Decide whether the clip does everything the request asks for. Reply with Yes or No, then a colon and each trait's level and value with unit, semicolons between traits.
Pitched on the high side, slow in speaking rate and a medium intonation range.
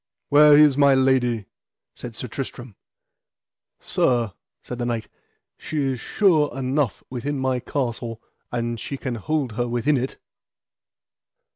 No: low, 130 Hz; slow, 130 wpm; average, 3.1 semitones